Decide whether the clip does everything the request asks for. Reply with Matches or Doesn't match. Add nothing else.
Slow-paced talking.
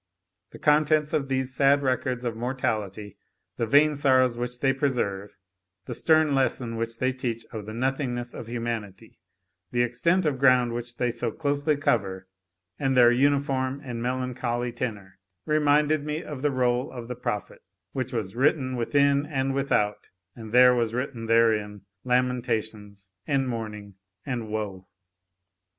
Doesn't match